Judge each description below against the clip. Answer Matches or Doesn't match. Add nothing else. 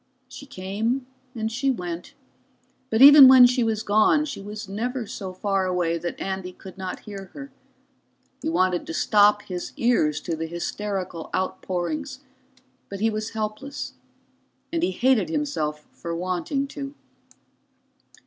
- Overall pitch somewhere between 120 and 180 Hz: Doesn't match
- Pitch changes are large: Matches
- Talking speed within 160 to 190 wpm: Doesn't match